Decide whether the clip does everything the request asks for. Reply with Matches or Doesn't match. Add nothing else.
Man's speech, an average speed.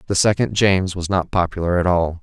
Doesn't match